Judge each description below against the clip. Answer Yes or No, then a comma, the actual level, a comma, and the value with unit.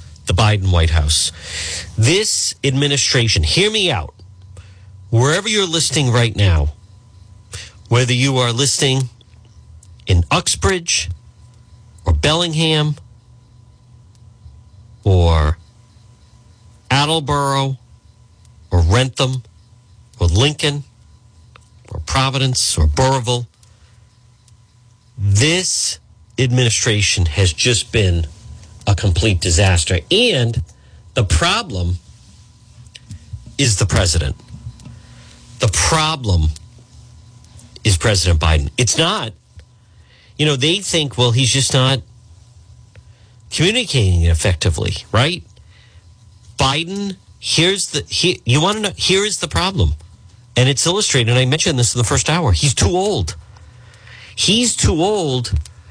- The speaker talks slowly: Yes, slow, 100 wpm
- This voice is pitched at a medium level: No, low, 110 Hz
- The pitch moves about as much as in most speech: Yes, average, 4.8 semitones